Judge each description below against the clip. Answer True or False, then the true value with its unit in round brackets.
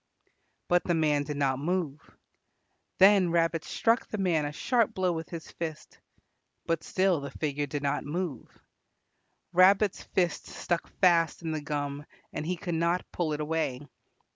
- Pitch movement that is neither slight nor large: True (3.4 semitones)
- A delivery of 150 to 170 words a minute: True (160 wpm)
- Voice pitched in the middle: True (165 Hz)